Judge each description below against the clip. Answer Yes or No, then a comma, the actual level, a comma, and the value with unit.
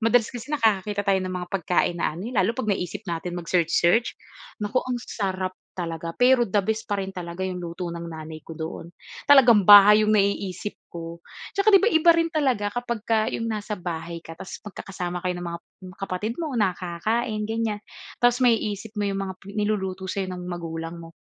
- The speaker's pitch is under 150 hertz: No, high, 195 Hz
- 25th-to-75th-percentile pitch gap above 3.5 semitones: Yes, average, 4.1 semitones